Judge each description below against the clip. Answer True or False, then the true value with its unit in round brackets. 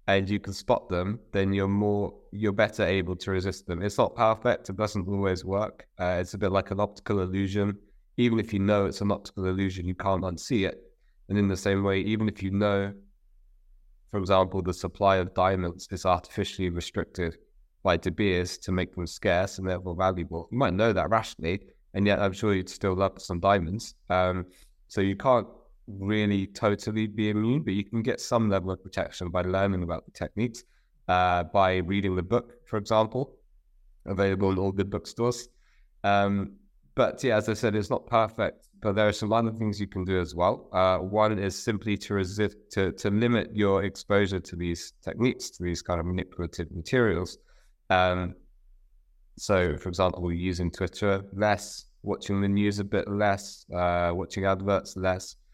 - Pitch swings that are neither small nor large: False (2.0 semitones)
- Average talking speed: True (185 wpm)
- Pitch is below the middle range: True (95 Hz)